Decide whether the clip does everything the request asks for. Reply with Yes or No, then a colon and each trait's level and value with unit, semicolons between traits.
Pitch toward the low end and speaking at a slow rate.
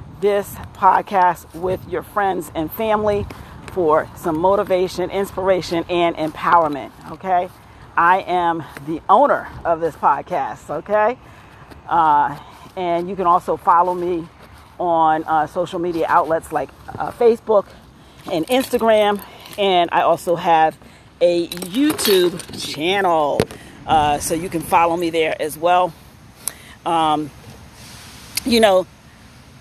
No: medium, 175 Hz; slow, 120 wpm